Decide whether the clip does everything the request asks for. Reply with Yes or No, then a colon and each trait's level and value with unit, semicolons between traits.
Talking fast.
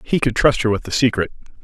Yes: fast, 255 wpm